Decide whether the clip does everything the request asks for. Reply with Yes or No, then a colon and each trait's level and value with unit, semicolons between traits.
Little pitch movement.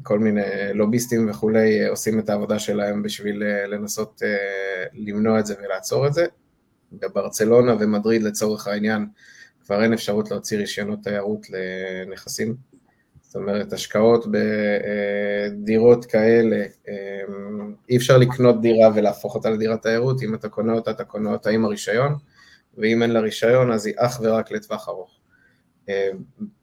Yes: narrow, 1.9 semitones